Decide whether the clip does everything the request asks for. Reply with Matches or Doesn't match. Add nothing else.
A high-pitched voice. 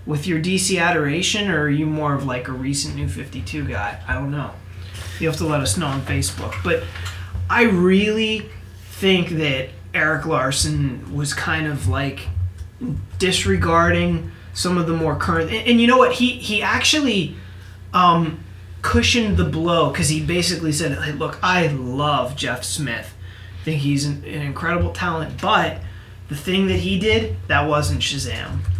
Doesn't match